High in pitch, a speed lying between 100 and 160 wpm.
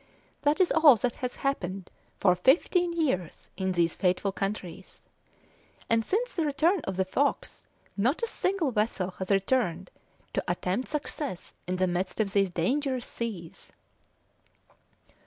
Yes: high, 210 Hz; average, 140 wpm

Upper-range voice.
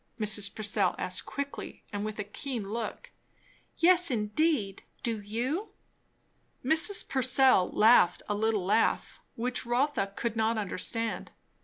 Yes: high, 225 Hz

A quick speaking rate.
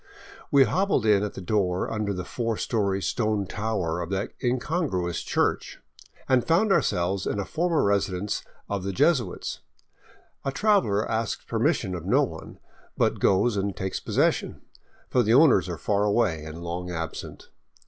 No: average, 160 wpm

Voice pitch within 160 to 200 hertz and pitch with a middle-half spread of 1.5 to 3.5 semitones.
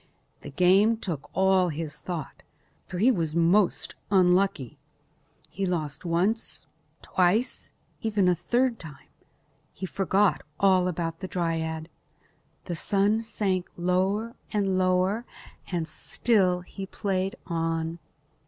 Yes: medium, 185 Hz; average, 2.9 semitones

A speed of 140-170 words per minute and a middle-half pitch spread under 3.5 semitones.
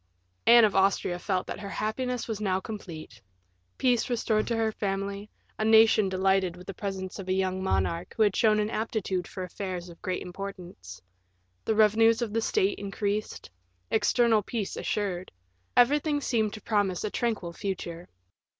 Yes: average, 165 wpm; average, 3.0 semitones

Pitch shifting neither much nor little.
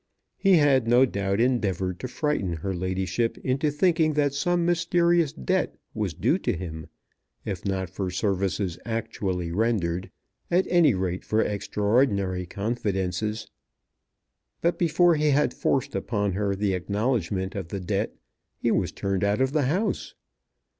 No: wide, 7.1 semitones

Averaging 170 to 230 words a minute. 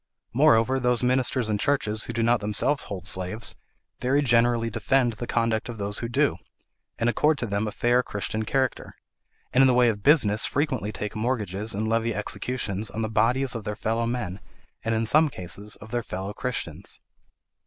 Yes: average, 185 wpm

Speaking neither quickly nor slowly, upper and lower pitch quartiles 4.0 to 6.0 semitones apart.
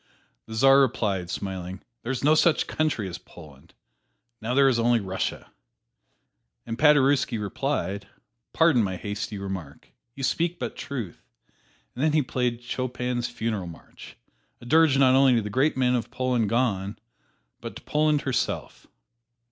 Yes: average, 150 wpm; average, 4.9 semitones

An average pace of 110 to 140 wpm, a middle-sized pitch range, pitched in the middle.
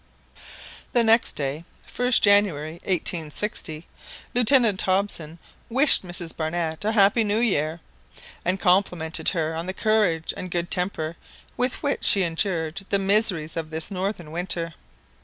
Yes: slow, 135 wpm; average, 4.2 semitones; medium, 180 Hz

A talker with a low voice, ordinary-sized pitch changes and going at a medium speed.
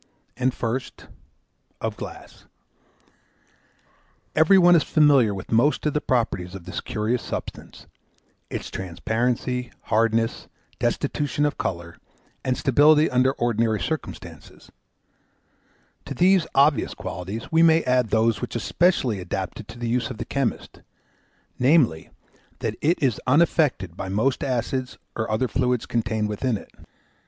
No: low, 125 Hz; average, 4.5 semitones; slow, 130 wpm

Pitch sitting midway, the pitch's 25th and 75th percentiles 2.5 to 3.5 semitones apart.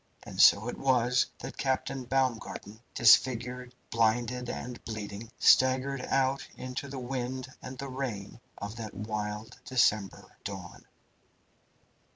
No: low, 125 Hz; average, 2.9 semitones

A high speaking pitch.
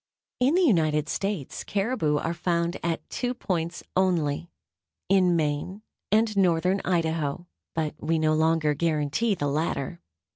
No: medium, 170 Hz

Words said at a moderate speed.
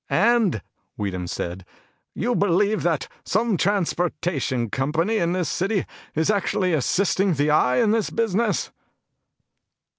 No: slow, 120 wpm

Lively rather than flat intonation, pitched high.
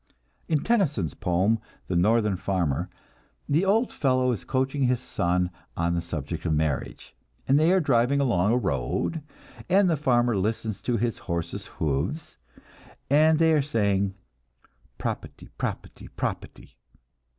No: wide, 8.3 semitones; low, 115 Hz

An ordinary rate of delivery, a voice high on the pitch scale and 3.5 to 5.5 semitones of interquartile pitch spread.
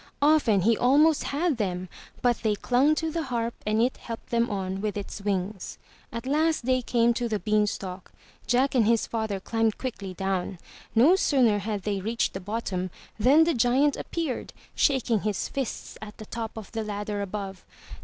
Yes: average, 180 wpm; high, 225 Hz; average, 3.9 semitones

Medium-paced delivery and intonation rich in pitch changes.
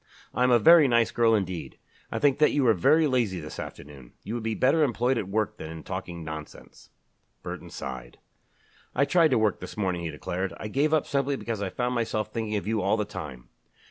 No: fast, 220 wpm; wide, 5.8 semitones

